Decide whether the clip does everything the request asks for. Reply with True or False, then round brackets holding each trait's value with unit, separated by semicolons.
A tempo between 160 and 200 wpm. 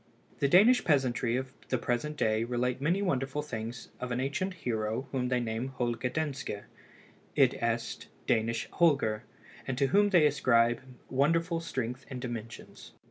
False (145 wpm)